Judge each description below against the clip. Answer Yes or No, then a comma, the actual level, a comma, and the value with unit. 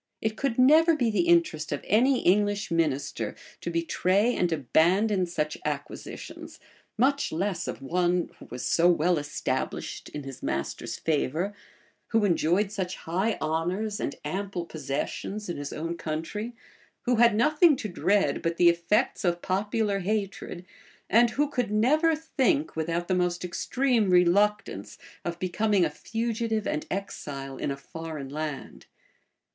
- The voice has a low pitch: No, medium, 180 Hz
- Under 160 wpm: Yes, average, 145 wpm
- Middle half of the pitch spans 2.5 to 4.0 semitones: No, average, 5.0 semitones